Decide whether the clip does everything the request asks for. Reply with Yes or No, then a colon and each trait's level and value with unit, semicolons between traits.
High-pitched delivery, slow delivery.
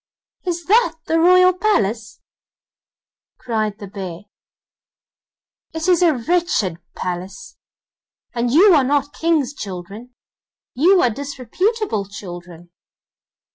Yes: very high, 260 Hz; slow, 100 wpm